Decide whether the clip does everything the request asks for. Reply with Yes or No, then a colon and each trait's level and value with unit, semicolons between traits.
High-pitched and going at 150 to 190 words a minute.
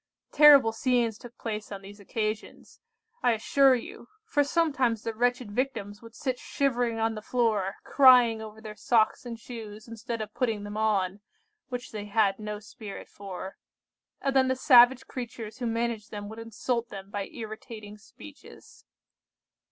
Yes: high, 225 Hz; average, 160 wpm